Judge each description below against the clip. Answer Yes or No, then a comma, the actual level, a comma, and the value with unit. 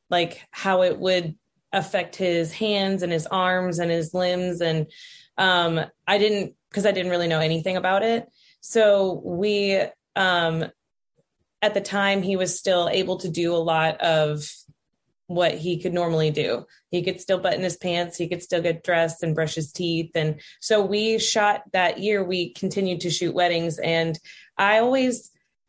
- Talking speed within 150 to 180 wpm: Yes, average, 175 wpm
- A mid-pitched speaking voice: Yes, medium, 180 Hz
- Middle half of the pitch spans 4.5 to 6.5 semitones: No, average, 2.7 semitones